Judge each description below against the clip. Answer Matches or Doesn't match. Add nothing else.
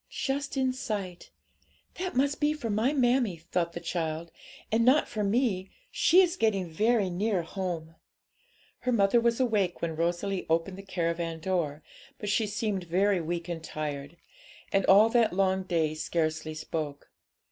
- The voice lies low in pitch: Doesn't match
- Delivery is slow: Doesn't match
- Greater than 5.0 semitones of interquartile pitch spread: Matches